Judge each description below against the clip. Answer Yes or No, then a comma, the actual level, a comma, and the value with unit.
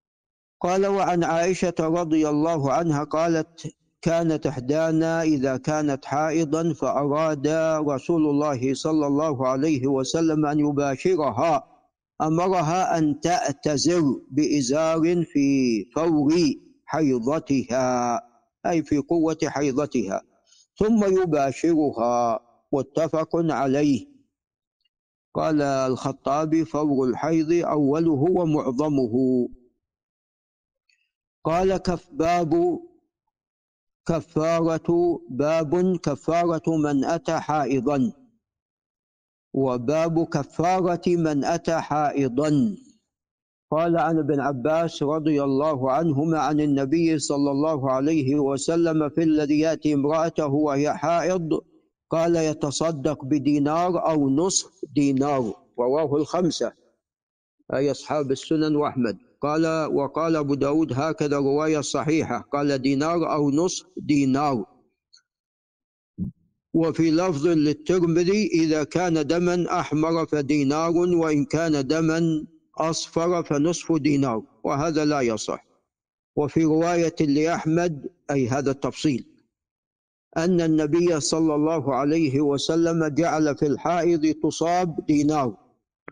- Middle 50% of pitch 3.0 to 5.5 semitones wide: No, narrow, 2.5 semitones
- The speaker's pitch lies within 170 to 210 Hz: No, medium, 155 Hz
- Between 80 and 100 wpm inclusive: Yes, average, 95 wpm